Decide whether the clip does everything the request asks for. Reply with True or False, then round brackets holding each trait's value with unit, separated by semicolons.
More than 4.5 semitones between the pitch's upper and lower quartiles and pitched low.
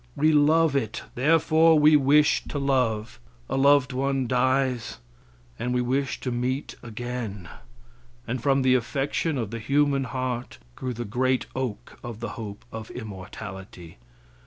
False (3.1 semitones; 130 Hz)